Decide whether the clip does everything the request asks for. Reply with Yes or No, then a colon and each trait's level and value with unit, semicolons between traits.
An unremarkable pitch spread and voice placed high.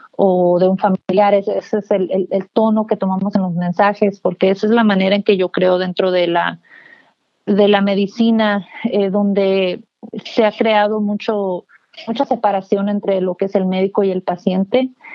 No: narrow, 2.1 semitones; high, 200 Hz